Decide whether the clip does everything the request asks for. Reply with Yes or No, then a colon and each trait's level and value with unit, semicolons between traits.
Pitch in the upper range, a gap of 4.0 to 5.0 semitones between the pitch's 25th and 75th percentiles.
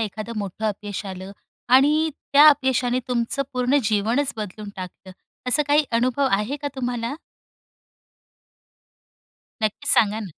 Yes: high, 235 Hz; average, 4.5 semitones